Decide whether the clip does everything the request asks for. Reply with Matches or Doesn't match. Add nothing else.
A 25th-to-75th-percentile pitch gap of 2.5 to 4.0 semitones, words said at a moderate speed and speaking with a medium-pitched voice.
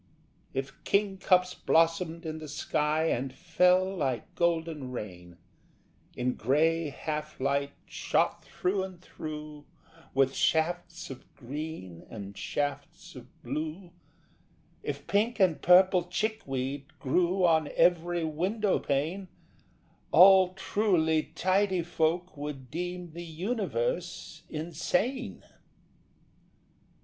Doesn't match